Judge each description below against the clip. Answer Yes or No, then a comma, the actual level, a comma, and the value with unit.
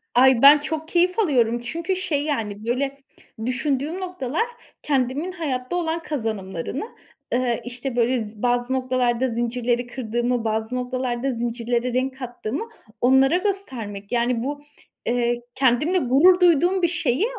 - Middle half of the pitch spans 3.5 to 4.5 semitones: Yes, average, 4.0 semitones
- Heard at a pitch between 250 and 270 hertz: Yes, very high, 255 Hz